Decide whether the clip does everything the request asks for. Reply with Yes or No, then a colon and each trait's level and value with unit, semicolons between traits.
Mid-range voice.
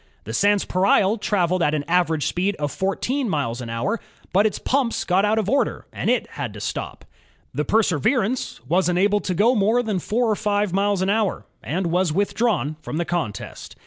No: high, 195 Hz